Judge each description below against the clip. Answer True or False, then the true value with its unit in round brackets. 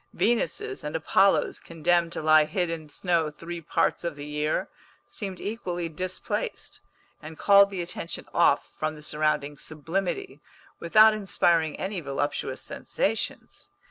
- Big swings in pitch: False (3.8 semitones)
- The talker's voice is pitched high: False (170 Hz)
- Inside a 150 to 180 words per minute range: False (135 wpm)